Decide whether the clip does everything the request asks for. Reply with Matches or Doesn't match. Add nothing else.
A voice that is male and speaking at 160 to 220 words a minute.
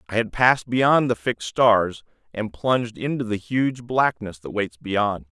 Matches